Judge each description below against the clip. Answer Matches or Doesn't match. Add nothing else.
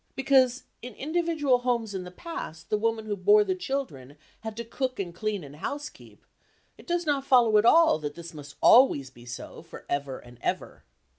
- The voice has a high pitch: Matches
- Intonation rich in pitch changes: Matches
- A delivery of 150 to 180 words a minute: Doesn't match